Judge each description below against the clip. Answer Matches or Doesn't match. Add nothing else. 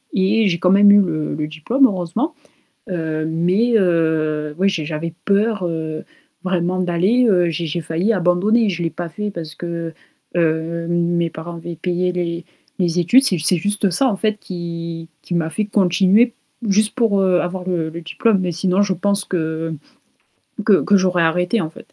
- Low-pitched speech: Doesn't match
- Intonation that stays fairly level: Doesn't match